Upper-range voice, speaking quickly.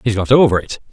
No: low, 110 Hz; fast, 260 wpm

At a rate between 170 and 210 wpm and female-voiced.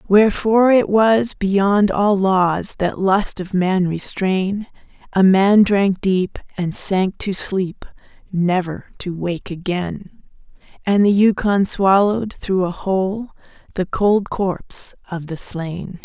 No: slow, 135 wpm; female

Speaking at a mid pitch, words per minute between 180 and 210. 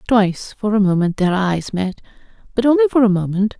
No: high, 210 Hz; average, 200 wpm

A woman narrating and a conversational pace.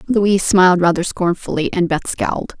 Yes: female; average, 160 wpm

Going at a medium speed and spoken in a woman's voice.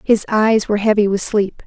No: fast, 215 wpm; female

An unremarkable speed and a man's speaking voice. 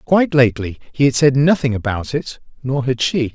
Yes: average, 180 wpm; male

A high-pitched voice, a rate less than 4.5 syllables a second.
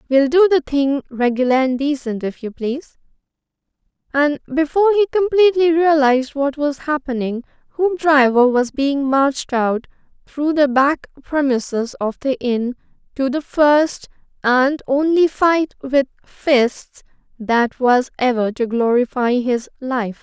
Yes: very high, 275 Hz; 4.2 syllables/s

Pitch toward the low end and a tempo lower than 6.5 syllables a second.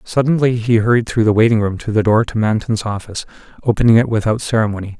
No: low, 110 Hz; 6.6 syllables/s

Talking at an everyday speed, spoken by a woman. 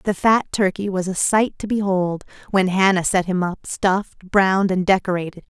Yes: average, 185 wpm; female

